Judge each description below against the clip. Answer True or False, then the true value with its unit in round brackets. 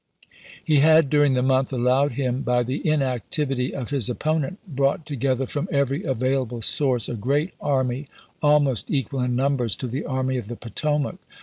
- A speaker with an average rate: True (175 wpm)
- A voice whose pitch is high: False (135 Hz)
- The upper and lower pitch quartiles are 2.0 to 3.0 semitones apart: True (2.5 semitones)